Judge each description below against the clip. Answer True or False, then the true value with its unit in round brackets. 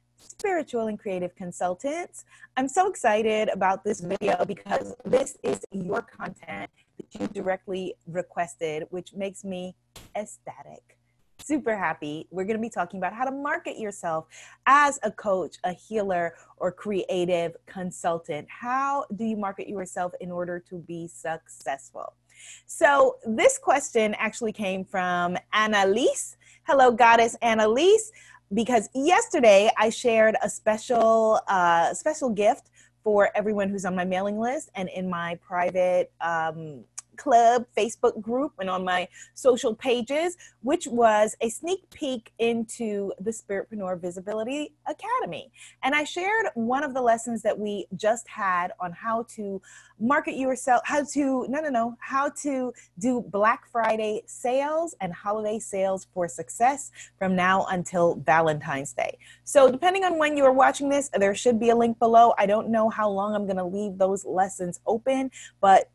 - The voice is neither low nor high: False (215 Hz)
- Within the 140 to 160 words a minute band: True (150 wpm)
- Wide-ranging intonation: True (5.9 semitones)